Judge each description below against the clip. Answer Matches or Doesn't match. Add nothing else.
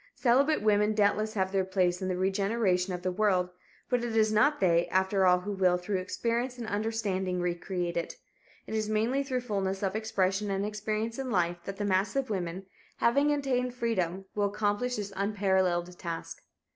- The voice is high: Matches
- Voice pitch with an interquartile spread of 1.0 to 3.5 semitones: Matches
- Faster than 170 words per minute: Matches